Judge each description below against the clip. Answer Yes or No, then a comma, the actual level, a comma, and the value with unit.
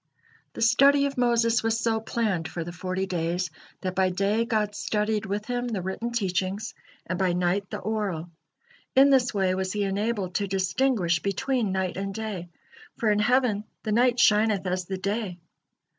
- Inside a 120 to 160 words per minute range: No, average, 175 wpm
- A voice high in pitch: Yes, high, 205 Hz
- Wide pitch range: No, average, 3.6 semitones